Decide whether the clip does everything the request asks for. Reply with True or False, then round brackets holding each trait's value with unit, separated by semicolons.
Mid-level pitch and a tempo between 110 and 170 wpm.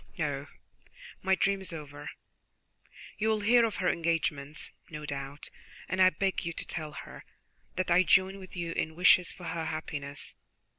True (170 Hz; 165 wpm)